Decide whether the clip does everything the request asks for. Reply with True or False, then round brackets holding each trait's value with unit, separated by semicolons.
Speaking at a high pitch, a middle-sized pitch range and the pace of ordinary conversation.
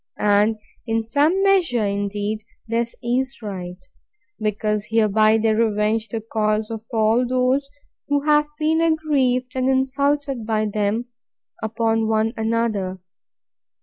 False (225 Hz; 3.5 semitones; 120 wpm)